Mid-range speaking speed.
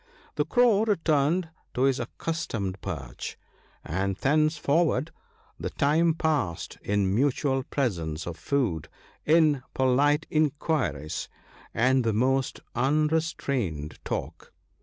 No: slow, 105 wpm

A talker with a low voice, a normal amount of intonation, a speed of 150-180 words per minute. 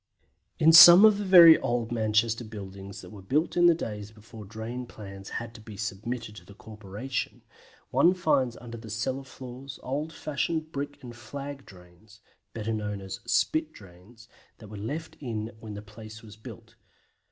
Yes: low, 115 Hz; average, 4.5 semitones; average, 175 wpm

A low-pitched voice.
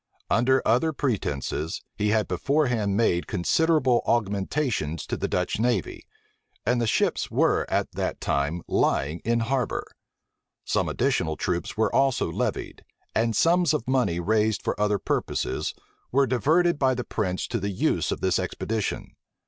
Yes: low, 115 Hz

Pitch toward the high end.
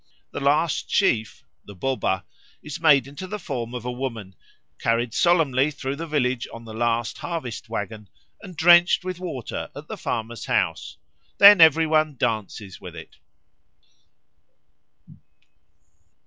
No: low, 135 Hz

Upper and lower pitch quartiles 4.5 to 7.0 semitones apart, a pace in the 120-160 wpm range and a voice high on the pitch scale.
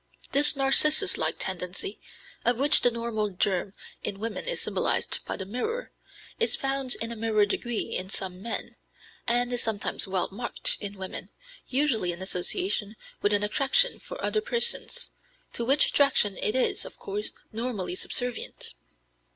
Yes: average, 5.3 semitones; average, 155 wpm; high, 230 Hz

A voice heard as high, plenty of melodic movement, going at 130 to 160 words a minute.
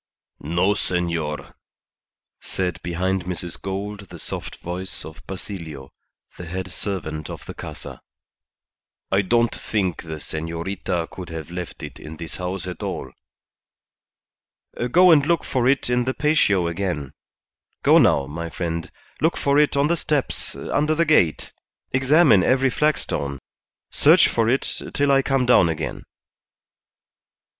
No: very low, 95 Hz; wide, 7.6 semitones; average, 140 wpm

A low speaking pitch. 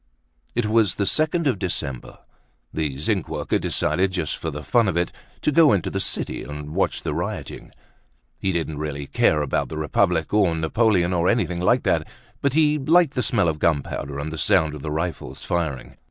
Yes: very low, 85 Hz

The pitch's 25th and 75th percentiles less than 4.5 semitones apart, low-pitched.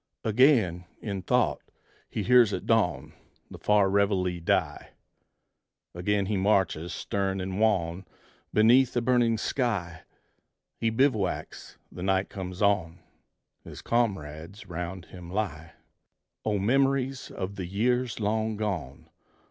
Yes: average, 3.8 semitones; low, 100 Hz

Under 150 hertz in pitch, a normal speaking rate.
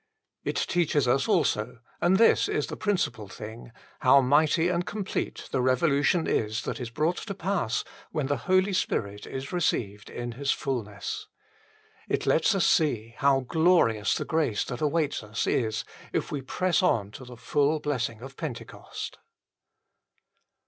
Yes: medium, 140 Hz; average, 155 wpm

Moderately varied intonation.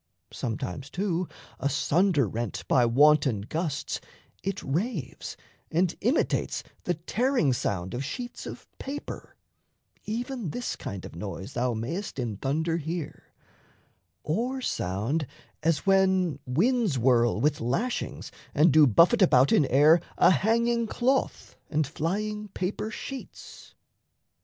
No: wide, 8.2 semitones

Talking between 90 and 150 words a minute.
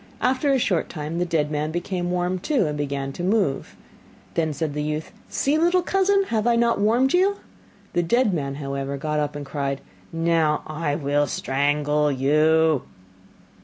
No: average, 170 wpm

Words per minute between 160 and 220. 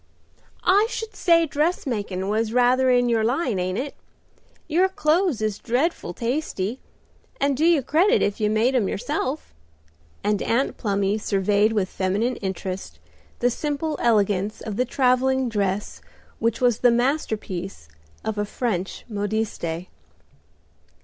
No: slow, 135 wpm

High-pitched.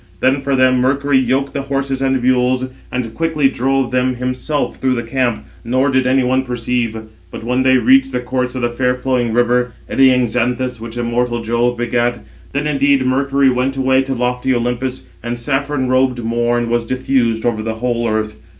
No: low, 125 Hz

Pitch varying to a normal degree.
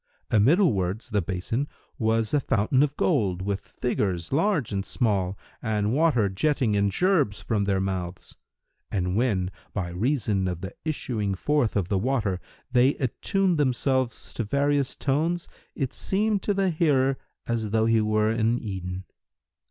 No: wide, 6.1 semitones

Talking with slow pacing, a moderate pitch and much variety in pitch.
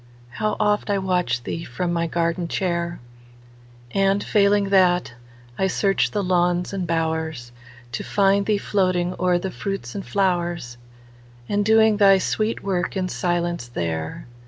Yes: slow, 130 wpm; medium, 175 Hz; wide, 8.3 semitones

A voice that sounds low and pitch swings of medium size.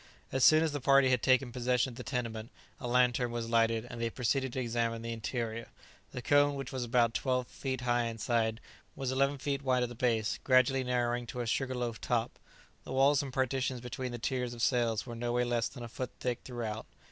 No: low, 125 Hz; narrow, 1.9 semitones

